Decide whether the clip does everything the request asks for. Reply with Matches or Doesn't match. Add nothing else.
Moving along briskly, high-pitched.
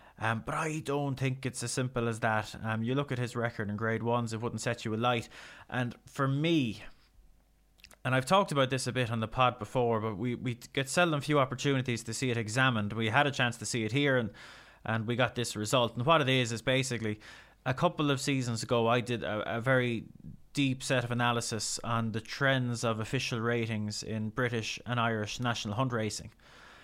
Doesn't match